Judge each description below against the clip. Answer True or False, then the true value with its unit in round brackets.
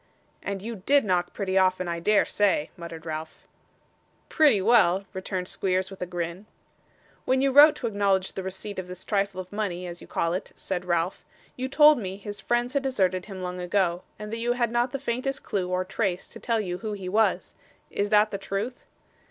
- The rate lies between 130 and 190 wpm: False (205 wpm)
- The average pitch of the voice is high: True (195 Hz)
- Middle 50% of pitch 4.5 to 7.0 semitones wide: False (3.7 semitones)